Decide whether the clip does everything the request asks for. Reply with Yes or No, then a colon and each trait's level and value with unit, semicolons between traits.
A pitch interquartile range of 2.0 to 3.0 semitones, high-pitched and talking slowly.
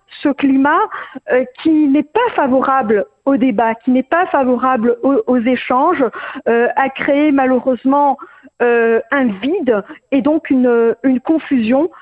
Yes: narrow, 2.6 semitones; very high, 265 Hz; slow, 135 wpm